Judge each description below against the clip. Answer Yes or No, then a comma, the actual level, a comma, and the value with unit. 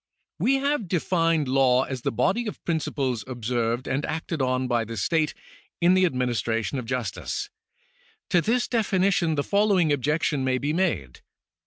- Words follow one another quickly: No, average, 155 wpm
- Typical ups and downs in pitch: No, wide, 6.3 semitones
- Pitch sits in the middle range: Yes, medium, 145 Hz